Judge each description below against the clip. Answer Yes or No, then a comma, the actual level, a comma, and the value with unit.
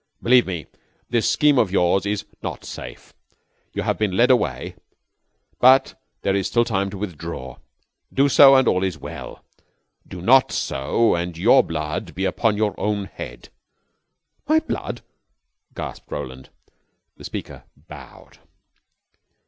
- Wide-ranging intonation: Yes, wide, 5.9 semitones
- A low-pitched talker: Yes, low, 100 Hz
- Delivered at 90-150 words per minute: Yes, average, 140 wpm